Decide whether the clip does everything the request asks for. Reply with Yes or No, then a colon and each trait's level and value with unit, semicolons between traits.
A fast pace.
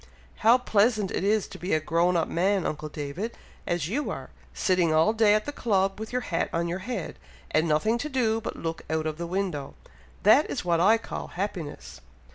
Yes: fast, 210 wpm